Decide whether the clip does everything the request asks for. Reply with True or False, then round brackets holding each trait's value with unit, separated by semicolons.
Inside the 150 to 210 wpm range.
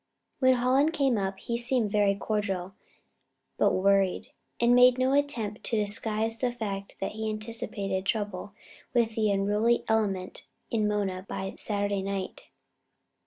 False (140 wpm)